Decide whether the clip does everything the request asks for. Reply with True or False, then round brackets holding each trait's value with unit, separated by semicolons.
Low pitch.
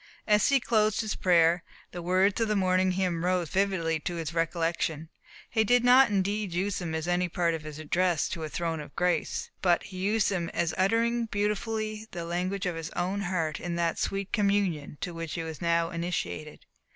False (180 Hz)